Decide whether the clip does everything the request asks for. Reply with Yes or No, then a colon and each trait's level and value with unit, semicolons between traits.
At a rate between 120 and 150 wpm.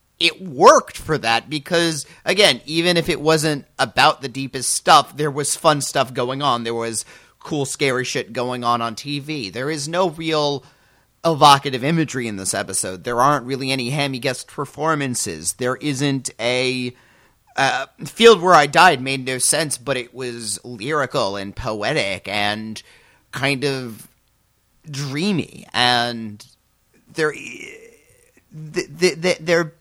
Yes: average, 140 wpm